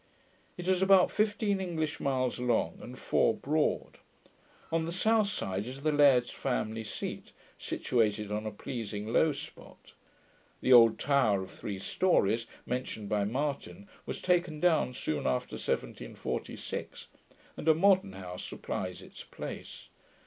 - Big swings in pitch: Yes, wide, 7.8 semitones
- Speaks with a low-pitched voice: Yes, low, 130 Hz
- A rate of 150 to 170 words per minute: No, average, 140 wpm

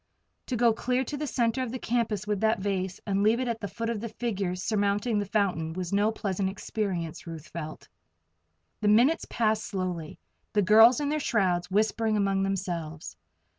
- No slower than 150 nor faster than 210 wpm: Yes, average, 185 wpm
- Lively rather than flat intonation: No, average, 3.5 semitones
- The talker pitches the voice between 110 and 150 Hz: No, high, 205 Hz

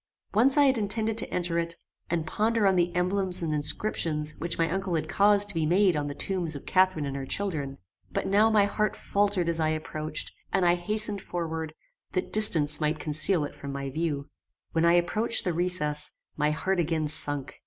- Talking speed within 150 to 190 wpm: No, average, 200 wpm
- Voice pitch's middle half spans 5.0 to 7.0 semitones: No, average, 4.5 semitones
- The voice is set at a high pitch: No, medium, 170 Hz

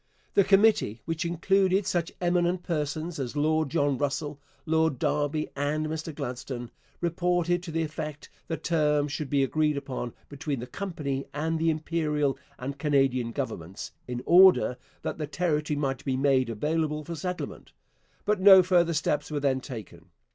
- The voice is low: No, medium, 150 Hz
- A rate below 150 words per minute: No, average, 155 wpm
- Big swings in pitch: No, average, 3.3 semitones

